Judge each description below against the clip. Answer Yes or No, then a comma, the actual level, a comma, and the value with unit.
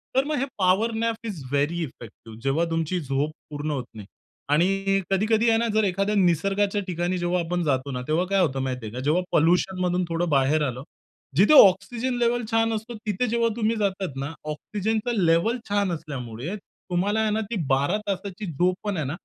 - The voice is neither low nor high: Yes, medium, 180 Hz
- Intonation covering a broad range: Yes, wide, 5.8 semitones